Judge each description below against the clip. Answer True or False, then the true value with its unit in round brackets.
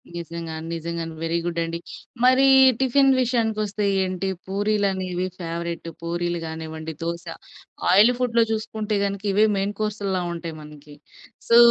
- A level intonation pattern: False (4.2 semitones)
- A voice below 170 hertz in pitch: False (185 Hz)